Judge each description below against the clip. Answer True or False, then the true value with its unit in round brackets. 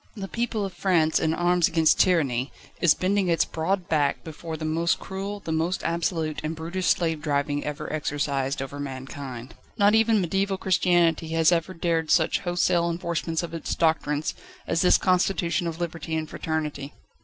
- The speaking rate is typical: True (165 wpm)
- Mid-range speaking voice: True (165 Hz)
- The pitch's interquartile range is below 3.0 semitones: True (2.6 semitones)